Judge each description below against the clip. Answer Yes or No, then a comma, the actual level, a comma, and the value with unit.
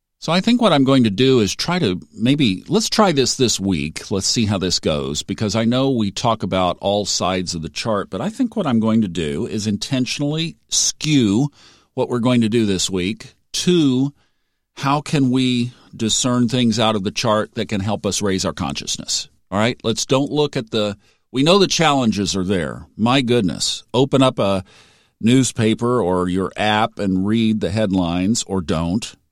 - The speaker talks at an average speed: Yes, average, 195 wpm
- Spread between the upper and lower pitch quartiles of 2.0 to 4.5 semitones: No, average, 5.1 semitones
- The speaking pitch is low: Yes, low, 110 Hz